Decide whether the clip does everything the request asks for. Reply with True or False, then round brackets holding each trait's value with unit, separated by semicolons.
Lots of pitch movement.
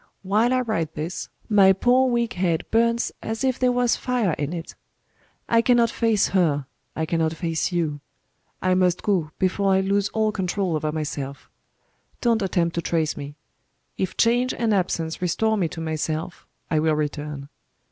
True (5.7 semitones)